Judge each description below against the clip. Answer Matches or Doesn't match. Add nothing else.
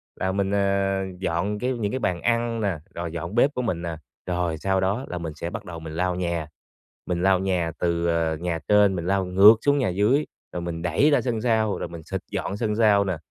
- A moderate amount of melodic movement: Matches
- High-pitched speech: Doesn't match